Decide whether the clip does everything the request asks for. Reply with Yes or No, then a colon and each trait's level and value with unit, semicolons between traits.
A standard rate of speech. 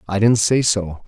No: fast, 220 wpm